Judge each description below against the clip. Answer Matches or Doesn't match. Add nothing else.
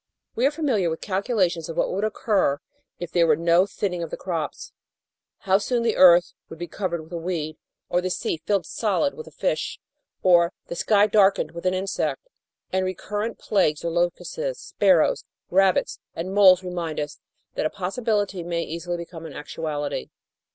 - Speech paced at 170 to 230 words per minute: Matches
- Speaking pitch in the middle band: Matches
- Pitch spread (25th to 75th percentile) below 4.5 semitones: Matches